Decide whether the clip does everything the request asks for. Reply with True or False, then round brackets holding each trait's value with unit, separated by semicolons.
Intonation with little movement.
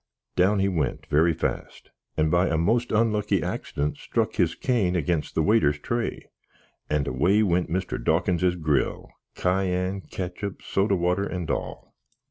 False (3.5 semitones)